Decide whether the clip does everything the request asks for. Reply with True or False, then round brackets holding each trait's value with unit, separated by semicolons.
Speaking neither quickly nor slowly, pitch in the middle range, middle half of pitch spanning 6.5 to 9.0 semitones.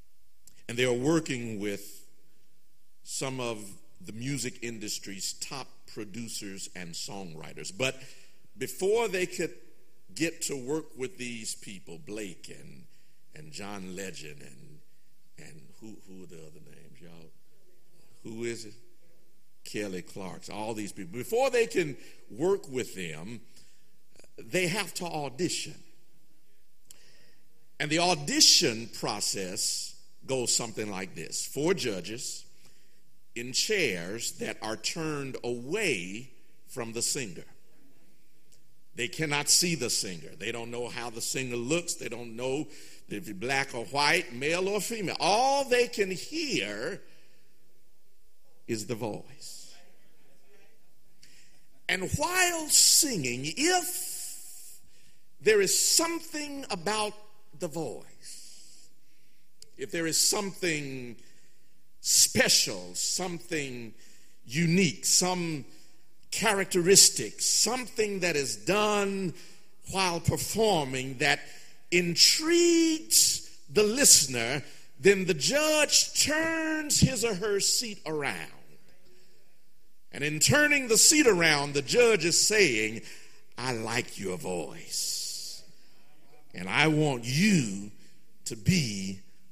False (110 wpm; 155 Hz; 8.4 semitones)